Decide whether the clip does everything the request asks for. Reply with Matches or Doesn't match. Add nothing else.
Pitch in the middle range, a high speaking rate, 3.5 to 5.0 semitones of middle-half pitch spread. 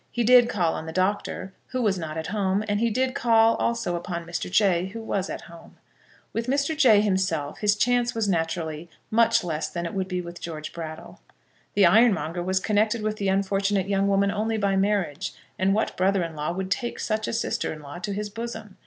Doesn't match